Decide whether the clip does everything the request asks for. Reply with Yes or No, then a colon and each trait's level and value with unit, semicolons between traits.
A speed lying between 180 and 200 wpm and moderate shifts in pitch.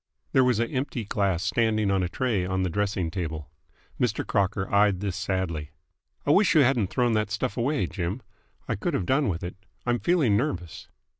Yes: average, 195 wpm; average, 4.7 semitones